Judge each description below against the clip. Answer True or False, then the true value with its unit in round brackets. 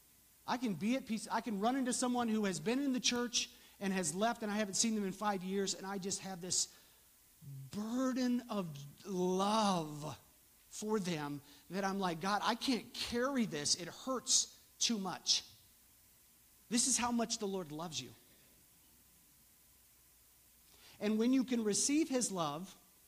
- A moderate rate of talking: True (165 wpm)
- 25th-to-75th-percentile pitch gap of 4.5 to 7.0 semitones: True (5.2 semitones)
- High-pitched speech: True (205 Hz)